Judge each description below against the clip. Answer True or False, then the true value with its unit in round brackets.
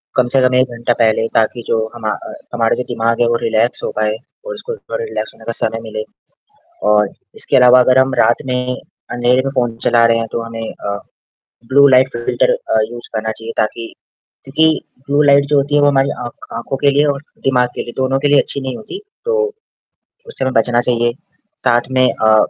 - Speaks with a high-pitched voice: False (125 Hz)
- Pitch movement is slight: False (3.0 semitones)